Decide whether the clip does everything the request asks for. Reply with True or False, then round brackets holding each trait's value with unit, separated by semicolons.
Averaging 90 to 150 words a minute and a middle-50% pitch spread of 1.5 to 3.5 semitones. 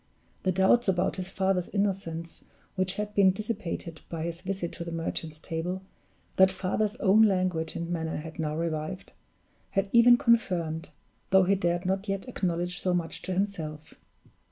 False (160 wpm; 2.8 semitones)